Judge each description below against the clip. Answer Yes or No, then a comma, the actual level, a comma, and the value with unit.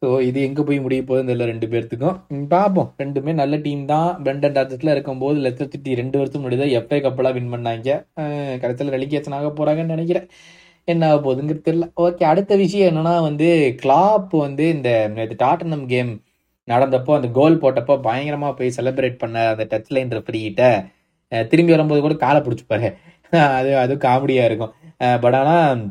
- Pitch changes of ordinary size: Yes, average, 3.8 semitones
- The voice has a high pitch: No, medium, 140 Hz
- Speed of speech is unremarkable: No, fast, 160 wpm